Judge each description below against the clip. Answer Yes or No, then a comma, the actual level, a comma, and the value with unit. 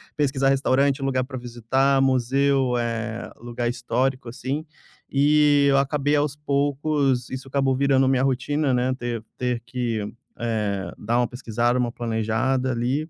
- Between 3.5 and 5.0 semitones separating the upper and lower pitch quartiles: No, narrow, 2.4 semitones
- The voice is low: Yes, low, 130 Hz